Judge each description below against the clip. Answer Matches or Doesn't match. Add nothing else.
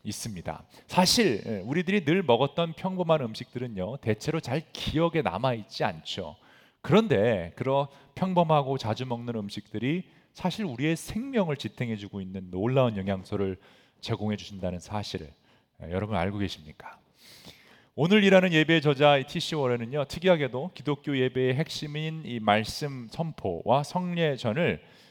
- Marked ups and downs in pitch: Matches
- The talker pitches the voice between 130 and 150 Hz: Matches